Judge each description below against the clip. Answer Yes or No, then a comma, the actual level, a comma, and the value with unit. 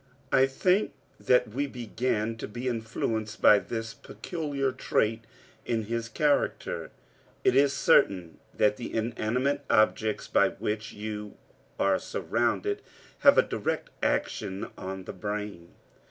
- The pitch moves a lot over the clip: No, average, 3.5 semitones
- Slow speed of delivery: Yes, slow, 125 wpm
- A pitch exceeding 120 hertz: No, low, 110 Hz